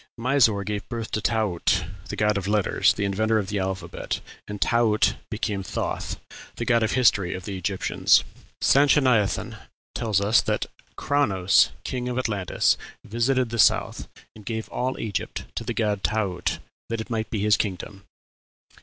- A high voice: No, low, 105 Hz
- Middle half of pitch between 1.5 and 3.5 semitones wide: Yes, average, 2.8 semitones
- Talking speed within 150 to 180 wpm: Yes, average, 160 wpm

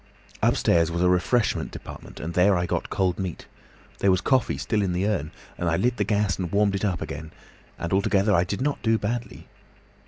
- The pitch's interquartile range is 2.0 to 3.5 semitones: Yes, average, 3.0 semitones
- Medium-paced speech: No, fast, 210 wpm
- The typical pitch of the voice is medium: No, very low, 95 Hz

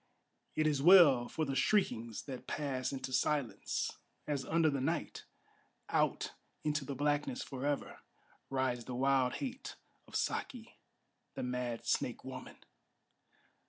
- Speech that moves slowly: Yes, slow, 125 wpm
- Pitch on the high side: No, medium, 140 Hz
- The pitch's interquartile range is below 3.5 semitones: Yes, average, 3.1 semitones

